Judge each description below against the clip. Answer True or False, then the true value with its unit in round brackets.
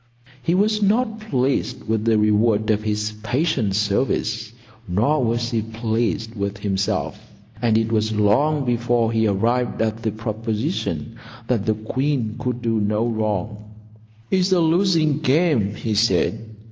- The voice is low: True (115 Hz)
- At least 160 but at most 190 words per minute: False (145 wpm)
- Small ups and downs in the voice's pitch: False (3.6 semitones)